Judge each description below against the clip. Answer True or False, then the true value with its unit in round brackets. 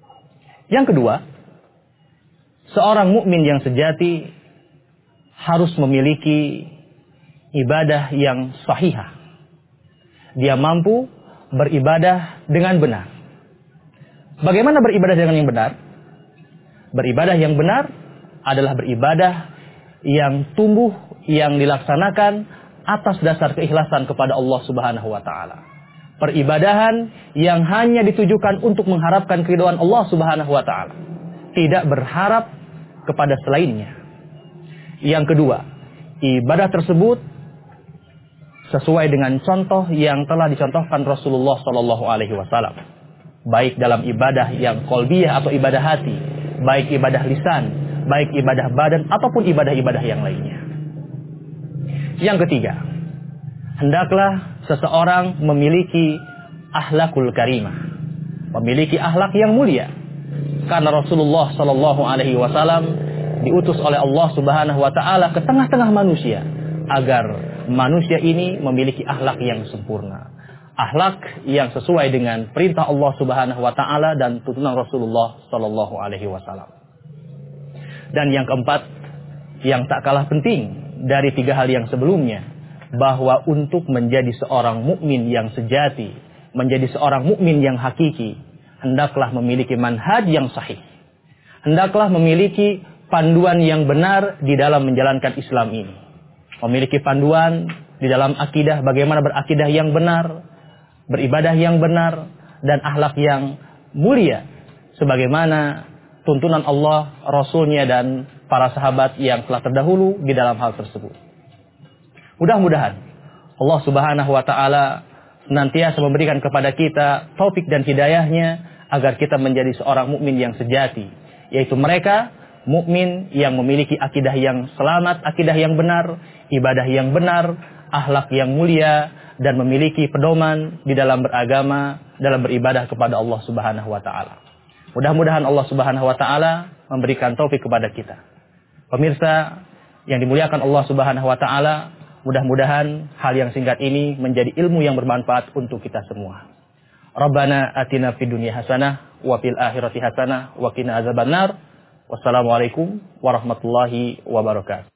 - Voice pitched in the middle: True (150 Hz)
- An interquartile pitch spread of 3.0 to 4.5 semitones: True (3.5 semitones)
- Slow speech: True (115 wpm)